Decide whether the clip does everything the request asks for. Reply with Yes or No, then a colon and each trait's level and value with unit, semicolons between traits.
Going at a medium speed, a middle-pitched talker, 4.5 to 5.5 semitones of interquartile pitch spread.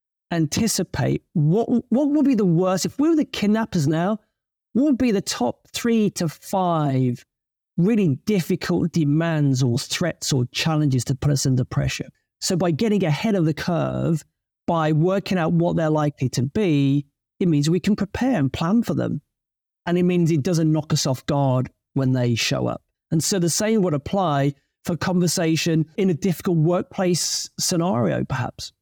Yes: average, 175 wpm; medium, 165 Hz; average, 4.8 semitones